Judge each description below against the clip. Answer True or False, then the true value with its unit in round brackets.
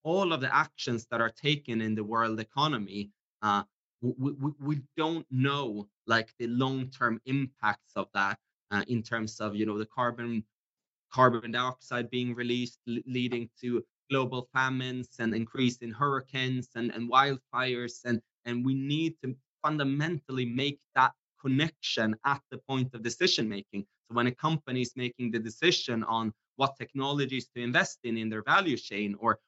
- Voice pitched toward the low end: True (125 Hz)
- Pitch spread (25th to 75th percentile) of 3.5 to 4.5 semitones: False (2.9 semitones)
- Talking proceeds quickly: False (165 wpm)